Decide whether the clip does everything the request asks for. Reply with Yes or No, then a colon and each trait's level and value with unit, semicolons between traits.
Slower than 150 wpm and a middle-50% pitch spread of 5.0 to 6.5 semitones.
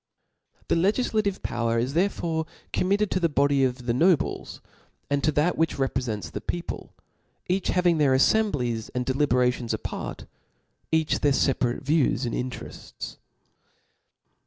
Yes: slow, 135 wpm; wide, 5.6 semitones